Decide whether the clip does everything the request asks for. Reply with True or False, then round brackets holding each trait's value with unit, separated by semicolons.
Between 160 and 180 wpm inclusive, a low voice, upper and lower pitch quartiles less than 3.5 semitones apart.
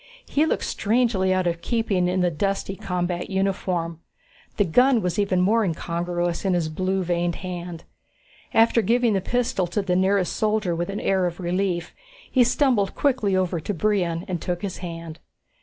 False (175 wpm; 185 Hz; 2.9 semitones)